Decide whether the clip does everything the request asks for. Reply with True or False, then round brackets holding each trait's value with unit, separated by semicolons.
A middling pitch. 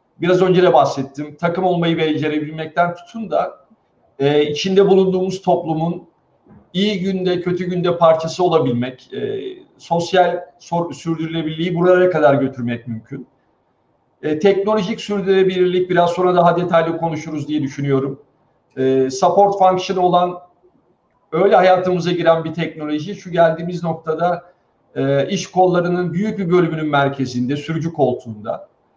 True (170 Hz)